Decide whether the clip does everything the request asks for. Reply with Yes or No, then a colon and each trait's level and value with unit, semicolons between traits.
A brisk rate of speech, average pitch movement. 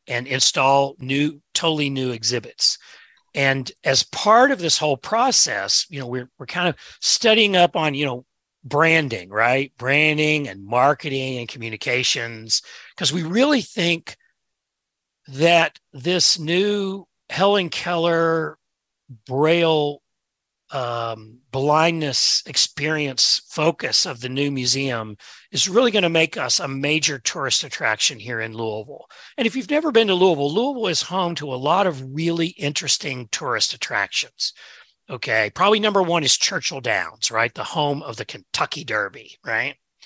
No: average, 140 wpm; average, 4.9 semitones